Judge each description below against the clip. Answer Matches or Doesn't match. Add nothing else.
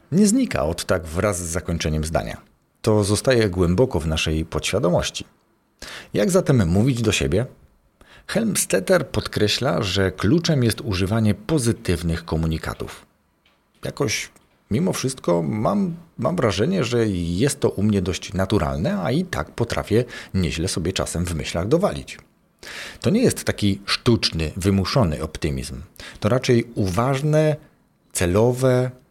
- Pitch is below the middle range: Matches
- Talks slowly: Doesn't match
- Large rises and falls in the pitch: Matches